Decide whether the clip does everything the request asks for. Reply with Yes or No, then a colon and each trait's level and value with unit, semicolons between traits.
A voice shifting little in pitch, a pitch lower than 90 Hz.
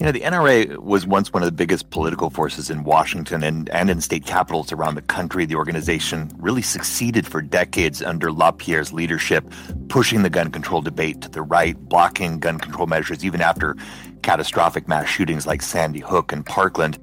Yes: narrow, 1.8 semitones; very low, 80 Hz